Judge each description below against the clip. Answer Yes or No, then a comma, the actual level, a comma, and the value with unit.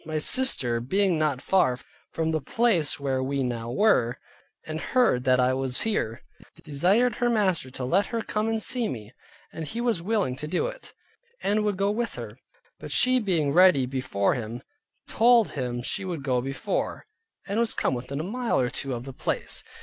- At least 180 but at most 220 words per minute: Yes, average, 190 wpm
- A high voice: No, medium, 155 Hz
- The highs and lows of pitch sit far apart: Yes, wide, 8.8 semitones